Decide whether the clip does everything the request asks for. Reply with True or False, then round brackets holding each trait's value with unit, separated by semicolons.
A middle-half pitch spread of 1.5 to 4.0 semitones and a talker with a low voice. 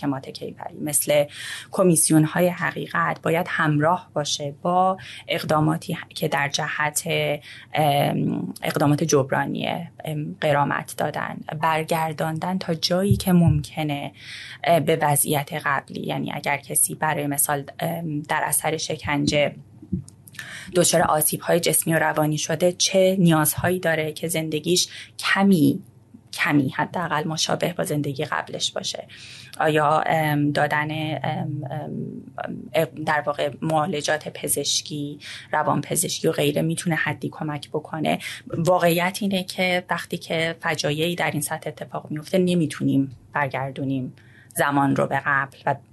False (2.4 semitones; 155 Hz)